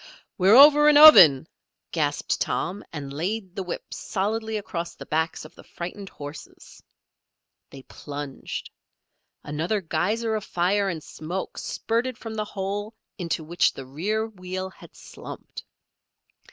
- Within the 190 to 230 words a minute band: No, slow, 135 wpm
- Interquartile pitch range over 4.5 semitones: Yes, average, 5.2 semitones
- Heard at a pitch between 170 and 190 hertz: Yes, medium, 185 Hz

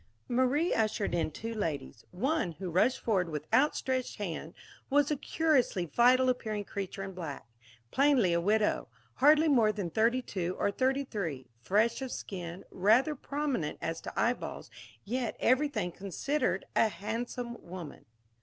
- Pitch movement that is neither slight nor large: No, wide, 6.3 semitones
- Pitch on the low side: No, high, 220 Hz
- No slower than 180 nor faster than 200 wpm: No, average, 145 wpm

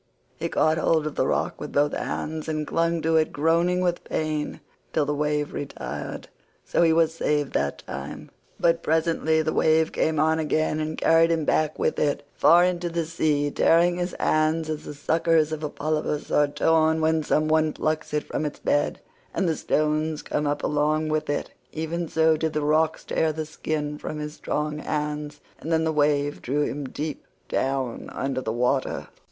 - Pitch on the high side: No, medium, 155 Hz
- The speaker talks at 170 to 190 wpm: Yes, average, 185 wpm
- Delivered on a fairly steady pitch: Yes, narrow, 1.4 semitones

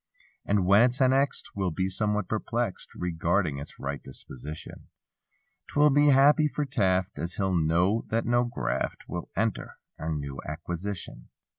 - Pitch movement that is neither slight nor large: No, wide, 6.5 semitones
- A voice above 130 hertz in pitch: No, very low, 95 Hz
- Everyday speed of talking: Yes, average, 145 wpm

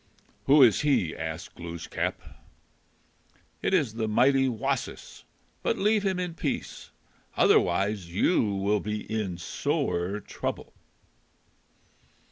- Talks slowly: Yes, slow, 105 wpm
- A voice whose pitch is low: Yes, low, 105 Hz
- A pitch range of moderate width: No, wide, 7.0 semitones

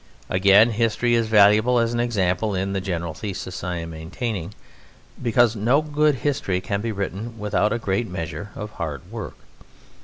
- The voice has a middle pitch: No, low, 105 Hz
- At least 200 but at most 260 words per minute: No, average, 165 wpm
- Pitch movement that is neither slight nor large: Yes, average, 4.0 semitones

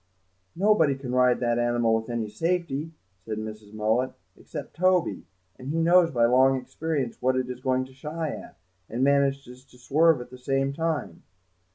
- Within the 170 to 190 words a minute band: Yes, average, 175 wpm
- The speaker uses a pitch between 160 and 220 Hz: No, low, 130 Hz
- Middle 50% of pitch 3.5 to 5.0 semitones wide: Yes, average, 4.3 semitones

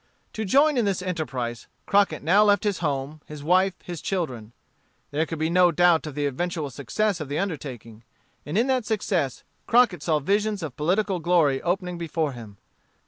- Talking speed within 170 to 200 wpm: Yes, average, 180 wpm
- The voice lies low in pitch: No, medium, 170 Hz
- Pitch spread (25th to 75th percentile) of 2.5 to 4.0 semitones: No, average, 5.3 semitones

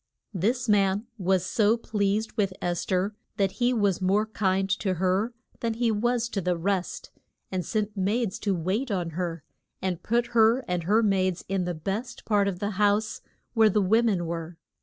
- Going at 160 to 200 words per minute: Yes, average, 185 wpm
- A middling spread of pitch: Yes, average, 3.1 semitones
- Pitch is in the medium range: No, high, 200 Hz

